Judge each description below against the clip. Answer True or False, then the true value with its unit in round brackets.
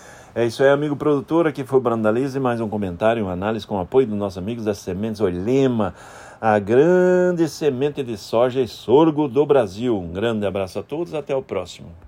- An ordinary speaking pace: False (200 wpm)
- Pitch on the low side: True (120 Hz)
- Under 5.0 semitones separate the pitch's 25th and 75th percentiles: False (5.3 semitones)